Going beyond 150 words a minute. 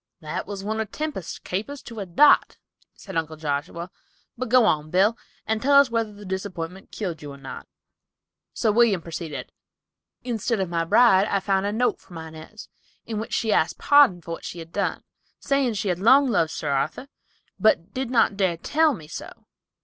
Yes: average, 190 wpm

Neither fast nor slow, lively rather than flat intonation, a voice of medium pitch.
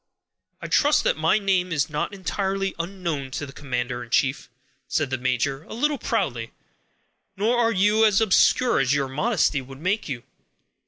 Yes: average, 170 wpm; wide, 7.1 semitones; medium, 165 Hz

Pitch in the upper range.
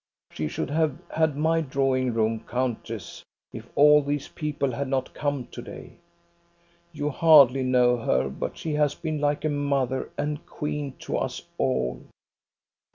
No: medium, 140 Hz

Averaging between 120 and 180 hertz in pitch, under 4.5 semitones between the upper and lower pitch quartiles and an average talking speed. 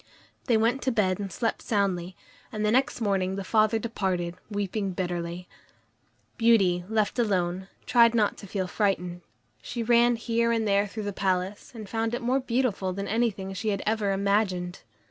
No: high, 205 Hz; average, 3.3 semitones; average, 170 wpm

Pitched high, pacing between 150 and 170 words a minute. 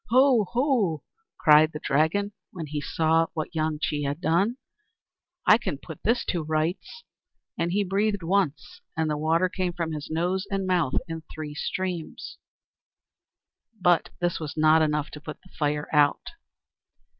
No: medium, 165 Hz; average, 160 wpm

